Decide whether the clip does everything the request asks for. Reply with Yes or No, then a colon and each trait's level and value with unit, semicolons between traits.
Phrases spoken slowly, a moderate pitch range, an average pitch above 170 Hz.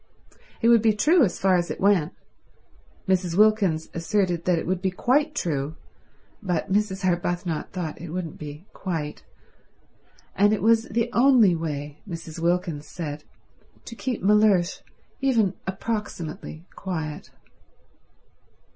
Yes: slow, 130 wpm; average, 4.3 semitones; medium, 185 Hz